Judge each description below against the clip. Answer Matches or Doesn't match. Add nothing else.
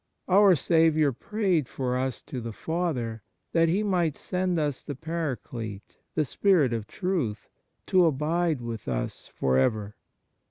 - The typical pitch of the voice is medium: Matches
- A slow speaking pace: Doesn't match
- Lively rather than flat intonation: Matches